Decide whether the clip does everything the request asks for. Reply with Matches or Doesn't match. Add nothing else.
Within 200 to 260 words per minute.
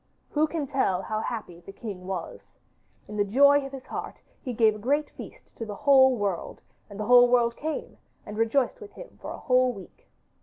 Matches